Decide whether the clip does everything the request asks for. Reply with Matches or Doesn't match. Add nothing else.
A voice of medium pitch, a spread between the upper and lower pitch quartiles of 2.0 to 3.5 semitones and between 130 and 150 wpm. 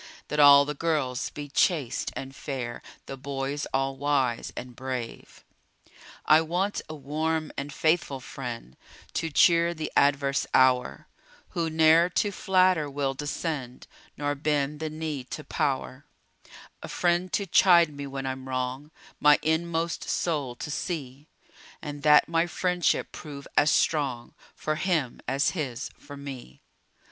Matches